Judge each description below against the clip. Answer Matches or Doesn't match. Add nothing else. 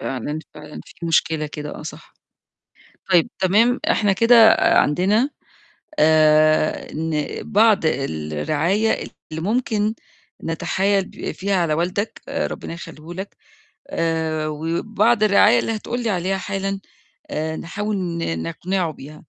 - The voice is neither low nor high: Matches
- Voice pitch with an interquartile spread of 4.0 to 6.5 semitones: Matches